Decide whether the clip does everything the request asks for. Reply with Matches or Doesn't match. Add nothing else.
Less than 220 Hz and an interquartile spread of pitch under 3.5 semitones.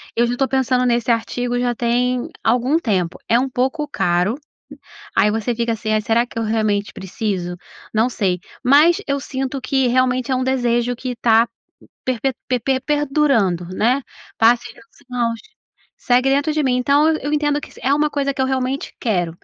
Doesn't match